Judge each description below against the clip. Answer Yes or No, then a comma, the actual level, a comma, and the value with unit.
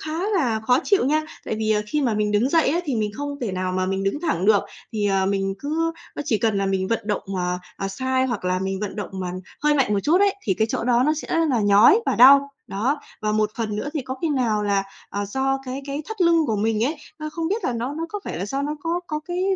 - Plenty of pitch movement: Yes, wide, 6.3 semitones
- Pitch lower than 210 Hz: No, high, 235 Hz